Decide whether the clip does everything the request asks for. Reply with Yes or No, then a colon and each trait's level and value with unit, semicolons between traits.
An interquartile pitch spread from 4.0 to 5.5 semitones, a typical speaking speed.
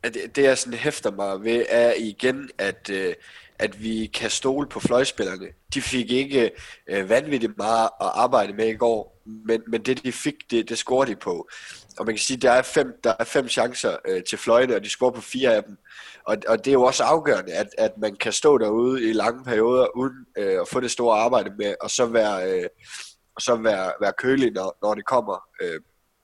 No: average, 3.6 semitones; average, 215 wpm